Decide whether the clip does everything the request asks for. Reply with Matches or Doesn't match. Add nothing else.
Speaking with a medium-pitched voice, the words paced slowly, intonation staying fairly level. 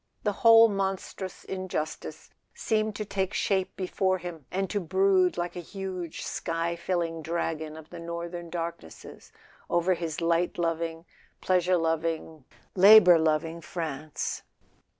Matches